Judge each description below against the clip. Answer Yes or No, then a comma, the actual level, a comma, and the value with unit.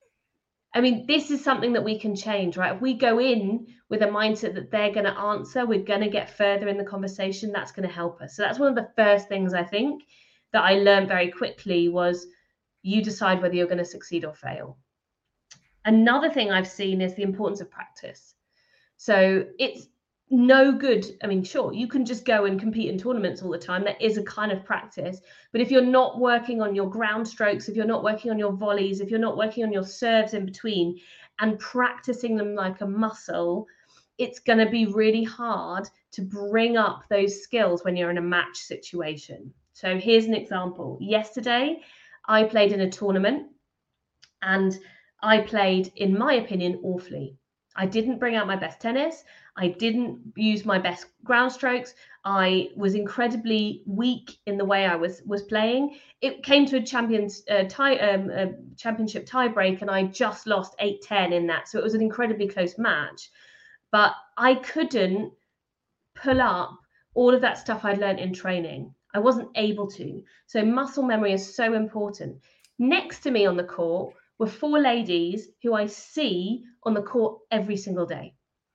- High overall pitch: Yes, high, 210 Hz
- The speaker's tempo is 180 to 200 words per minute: Yes, average, 190 wpm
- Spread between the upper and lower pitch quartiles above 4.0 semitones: No, average, 3.7 semitones